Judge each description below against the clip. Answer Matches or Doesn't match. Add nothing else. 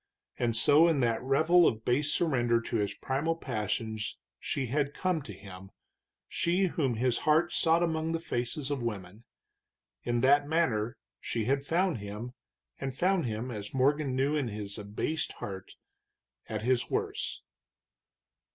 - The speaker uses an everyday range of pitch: Doesn't match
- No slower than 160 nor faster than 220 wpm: Doesn't match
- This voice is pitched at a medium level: Doesn't match